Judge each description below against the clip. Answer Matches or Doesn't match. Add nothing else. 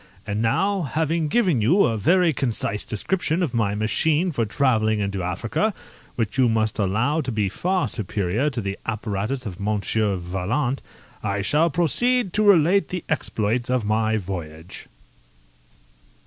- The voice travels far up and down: Matches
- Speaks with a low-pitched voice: Matches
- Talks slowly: Doesn't match